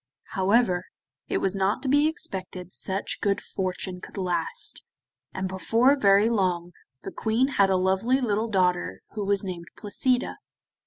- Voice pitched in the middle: No, high, 195 Hz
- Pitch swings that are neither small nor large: Yes, average, 3.7 semitones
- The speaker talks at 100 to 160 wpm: Yes, average, 150 wpm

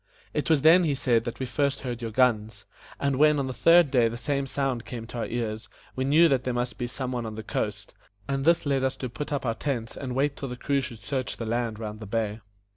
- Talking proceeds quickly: Yes, fast, 265 wpm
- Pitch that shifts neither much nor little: Yes, average, 3.3 semitones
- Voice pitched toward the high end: No, low, 125 Hz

